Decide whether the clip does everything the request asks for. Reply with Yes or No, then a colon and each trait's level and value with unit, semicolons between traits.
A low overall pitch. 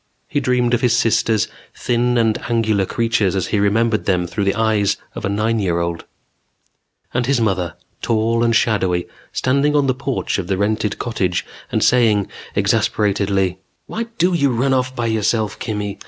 Yes: low, 110 Hz